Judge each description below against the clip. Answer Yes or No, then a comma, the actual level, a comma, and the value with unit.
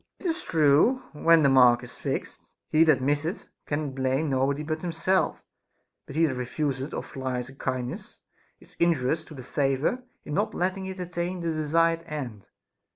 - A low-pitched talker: No, medium, 150 Hz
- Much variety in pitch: No, average, 3.9 semitones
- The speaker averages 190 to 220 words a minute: No, average, 170 wpm